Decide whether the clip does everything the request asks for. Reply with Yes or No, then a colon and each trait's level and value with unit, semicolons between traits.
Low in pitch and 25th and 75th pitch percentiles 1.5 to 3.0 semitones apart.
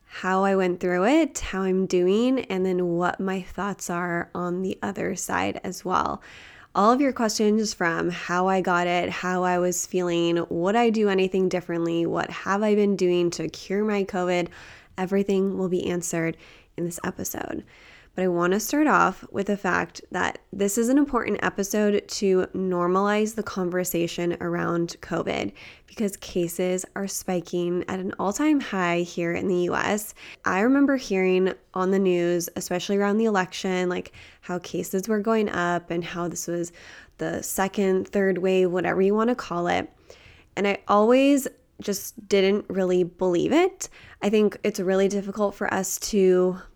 No: medium, 185 Hz; narrow, 2.5 semitones